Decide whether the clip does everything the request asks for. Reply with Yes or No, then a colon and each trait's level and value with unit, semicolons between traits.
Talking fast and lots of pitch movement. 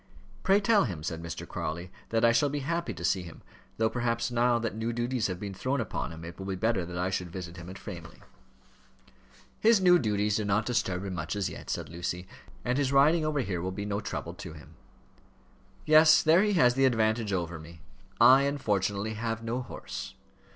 Yes: fast, 210 wpm; wide, 6.2 semitones